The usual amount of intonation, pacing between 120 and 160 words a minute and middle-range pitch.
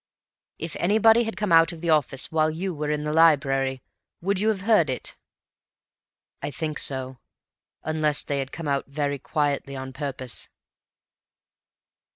Yes: average, 3.4 semitones; average, 155 wpm; medium, 150 Hz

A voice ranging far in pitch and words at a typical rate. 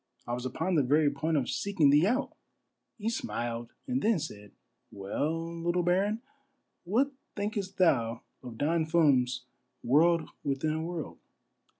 Yes: wide, 6.0 semitones; average, 155 wpm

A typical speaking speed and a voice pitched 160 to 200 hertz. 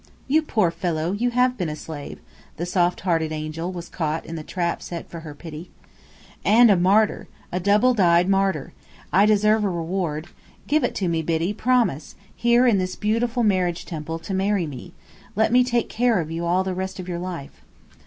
Yes: average, 195 wpm; medium, 185 Hz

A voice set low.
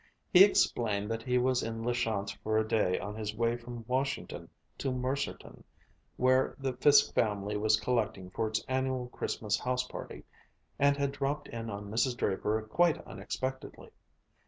Yes: low, 120 Hz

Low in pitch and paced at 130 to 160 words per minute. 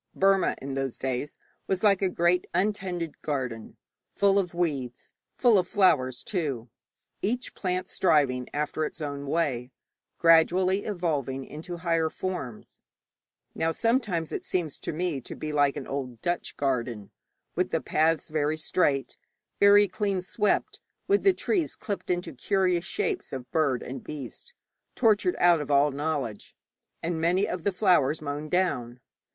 No: medium, 165 Hz; average, 150 wpm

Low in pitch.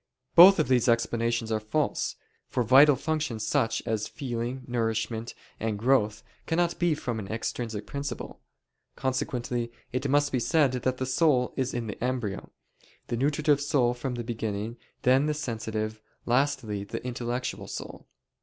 Yes: low, 125 Hz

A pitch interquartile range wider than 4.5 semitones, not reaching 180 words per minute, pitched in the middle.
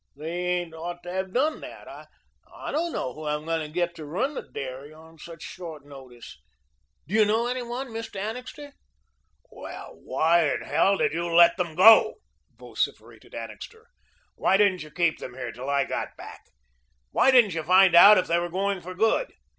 No: average, 5.1 semitones; average, 185 wpm; medium, 175 Hz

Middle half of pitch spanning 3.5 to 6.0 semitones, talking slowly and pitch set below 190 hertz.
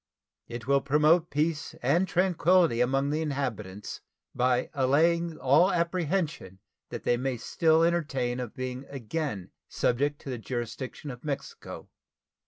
Yes: average, 4.7 semitones; slow, 130 wpm; medium, 140 Hz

